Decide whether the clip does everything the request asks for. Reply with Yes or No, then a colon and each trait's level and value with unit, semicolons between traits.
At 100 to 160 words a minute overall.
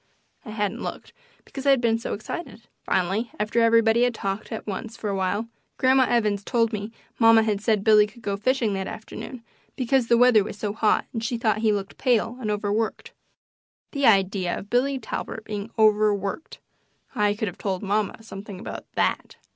No: average, 185 wpm